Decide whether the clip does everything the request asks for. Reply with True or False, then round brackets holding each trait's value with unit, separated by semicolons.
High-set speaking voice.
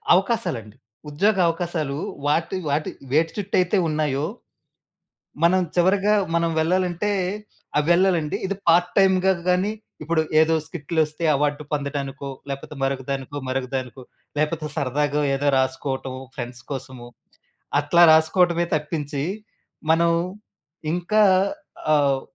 False (155 Hz)